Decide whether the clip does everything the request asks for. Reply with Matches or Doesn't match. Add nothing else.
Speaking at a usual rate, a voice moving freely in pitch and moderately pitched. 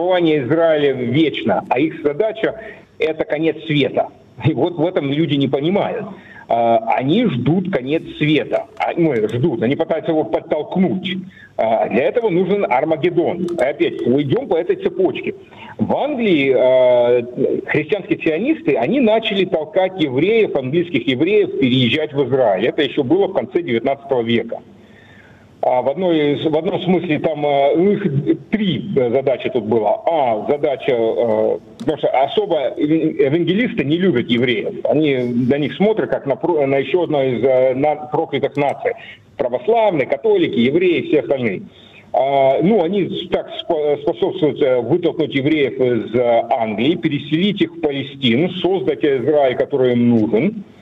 Matches